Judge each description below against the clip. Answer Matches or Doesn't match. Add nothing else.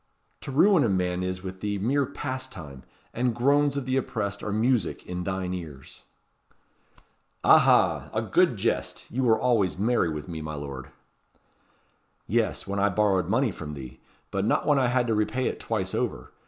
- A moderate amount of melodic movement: Doesn't match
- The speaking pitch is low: Matches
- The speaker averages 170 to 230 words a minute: Matches